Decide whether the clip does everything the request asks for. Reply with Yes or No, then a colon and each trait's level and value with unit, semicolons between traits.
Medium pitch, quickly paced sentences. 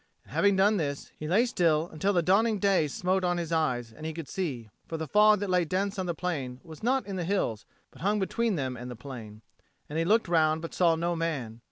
Yes: medium, 170 Hz; fast, 245 wpm